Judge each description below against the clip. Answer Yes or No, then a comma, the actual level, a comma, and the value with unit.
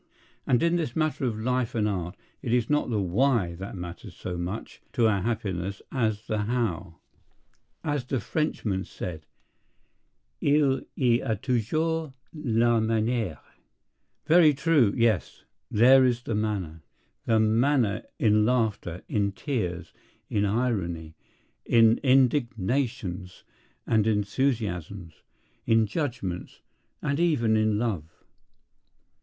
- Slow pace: Yes, slow, 115 wpm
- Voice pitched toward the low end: Yes, low, 110 Hz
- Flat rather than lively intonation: No, average, 4.4 semitones